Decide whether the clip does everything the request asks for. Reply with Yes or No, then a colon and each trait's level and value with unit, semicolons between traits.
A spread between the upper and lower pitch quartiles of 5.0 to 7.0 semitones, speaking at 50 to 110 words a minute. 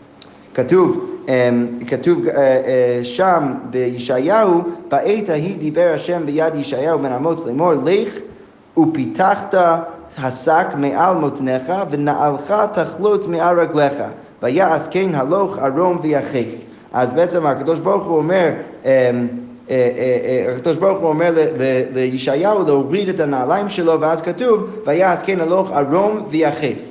Yes: wide, 5.5 semitones; average, 105 wpm